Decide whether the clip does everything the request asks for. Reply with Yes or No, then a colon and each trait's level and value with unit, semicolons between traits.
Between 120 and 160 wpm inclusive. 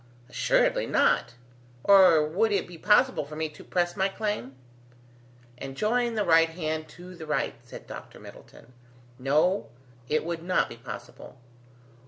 Yes: average, 150 wpm